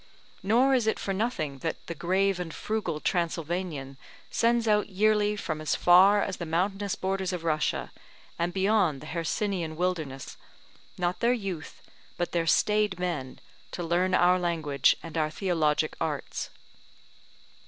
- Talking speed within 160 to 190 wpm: No, average, 145 wpm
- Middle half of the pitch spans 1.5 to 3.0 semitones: No, average, 3.6 semitones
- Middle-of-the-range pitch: Yes, medium, 180 Hz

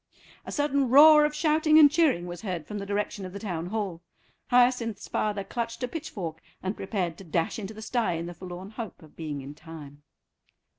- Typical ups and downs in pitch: No, wide, 6.2 semitones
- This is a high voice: Yes, high, 200 Hz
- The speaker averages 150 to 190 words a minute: No, average, 200 wpm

